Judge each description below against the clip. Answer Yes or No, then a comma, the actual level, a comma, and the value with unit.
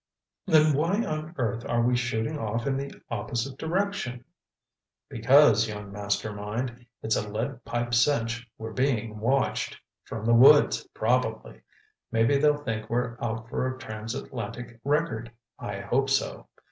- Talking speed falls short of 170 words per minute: Yes, average, 140 wpm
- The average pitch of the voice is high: No, low, 120 Hz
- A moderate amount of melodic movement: Yes, average, 3.5 semitones